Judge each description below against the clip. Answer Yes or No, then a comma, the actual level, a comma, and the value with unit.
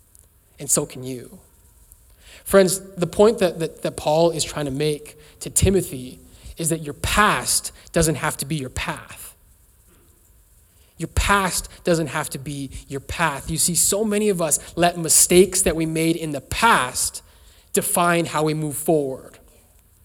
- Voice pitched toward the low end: No, medium, 150 Hz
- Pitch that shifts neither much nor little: No, wide, 6.7 semitones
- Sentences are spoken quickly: No, average, 160 wpm